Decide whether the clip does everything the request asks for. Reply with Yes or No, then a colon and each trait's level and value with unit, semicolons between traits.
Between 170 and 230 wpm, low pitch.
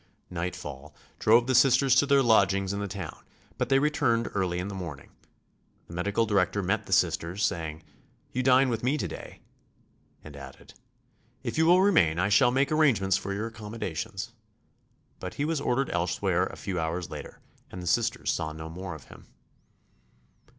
Yes: average, 175 wpm; low, 100 Hz